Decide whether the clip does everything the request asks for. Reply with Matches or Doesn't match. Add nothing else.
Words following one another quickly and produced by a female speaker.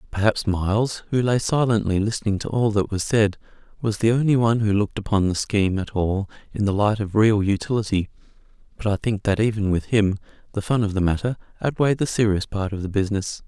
Doesn't match